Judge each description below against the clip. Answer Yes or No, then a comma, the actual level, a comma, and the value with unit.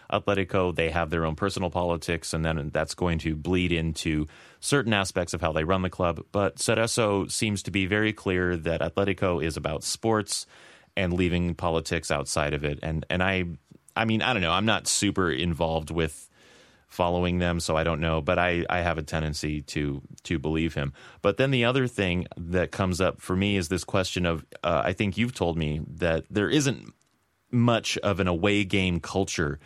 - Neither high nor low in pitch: No, very low, 90 Hz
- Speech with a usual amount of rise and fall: Yes, average, 3.4 semitones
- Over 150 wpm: Yes, average, 200 wpm